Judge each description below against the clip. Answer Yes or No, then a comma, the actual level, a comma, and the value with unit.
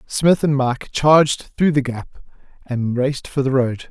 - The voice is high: No, low, 135 Hz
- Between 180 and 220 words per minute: Yes, average, 200 wpm